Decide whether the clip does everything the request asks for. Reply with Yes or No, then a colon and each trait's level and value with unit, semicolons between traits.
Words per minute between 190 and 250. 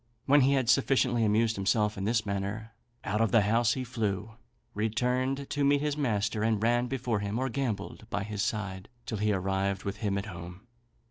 Yes: average, 195 wpm